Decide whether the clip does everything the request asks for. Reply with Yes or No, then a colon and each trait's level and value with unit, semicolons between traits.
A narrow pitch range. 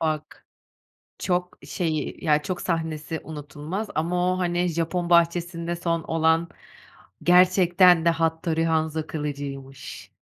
Yes: narrow, 1.9 semitones